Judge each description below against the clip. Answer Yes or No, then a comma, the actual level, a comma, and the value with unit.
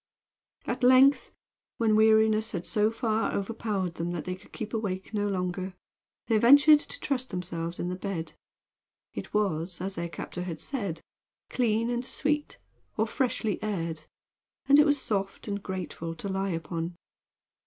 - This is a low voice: No, high, 200 Hz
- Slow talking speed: No, average, 155 wpm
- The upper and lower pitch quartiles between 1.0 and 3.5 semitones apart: No, average, 4.2 semitones